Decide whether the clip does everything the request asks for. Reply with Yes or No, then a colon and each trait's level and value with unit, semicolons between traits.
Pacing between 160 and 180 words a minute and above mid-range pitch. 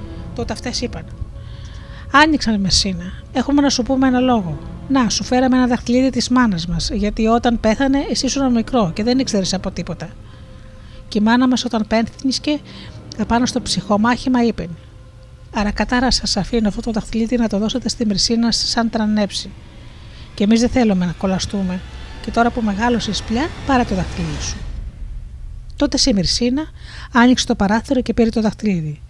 Yes: average, 165 wpm; high, 225 Hz